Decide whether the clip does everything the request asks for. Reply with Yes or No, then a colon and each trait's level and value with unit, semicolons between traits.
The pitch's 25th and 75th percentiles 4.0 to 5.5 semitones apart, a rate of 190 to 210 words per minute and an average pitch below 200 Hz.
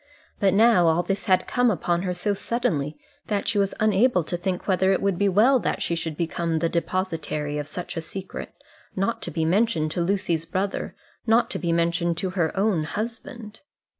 No: average, 3.4 semitones; average, 195 wpm; medium, 185 Hz